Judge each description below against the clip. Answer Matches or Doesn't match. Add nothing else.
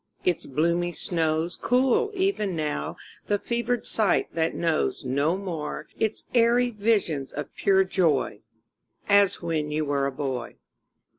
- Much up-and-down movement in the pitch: Matches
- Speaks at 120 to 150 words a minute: Matches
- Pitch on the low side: Doesn't match